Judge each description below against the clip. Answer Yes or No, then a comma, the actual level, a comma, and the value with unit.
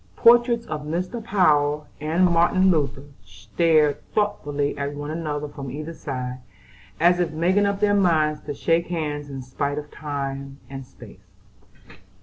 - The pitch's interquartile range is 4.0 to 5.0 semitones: No, average, 3.6 semitones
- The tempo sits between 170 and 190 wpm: No, average, 145 wpm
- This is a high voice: No, medium, 150 Hz